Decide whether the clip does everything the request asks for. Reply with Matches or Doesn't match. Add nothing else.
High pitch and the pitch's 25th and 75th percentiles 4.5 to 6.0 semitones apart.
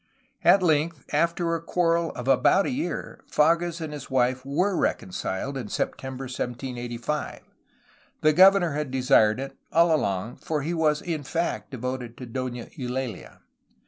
Doesn't match